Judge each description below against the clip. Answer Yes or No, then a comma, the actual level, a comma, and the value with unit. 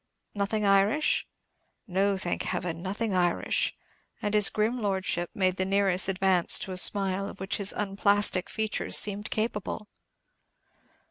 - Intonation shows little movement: Yes, narrow, 1.8 semitones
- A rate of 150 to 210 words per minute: No, slow, 135 wpm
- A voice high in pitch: Yes, high, 195 Hz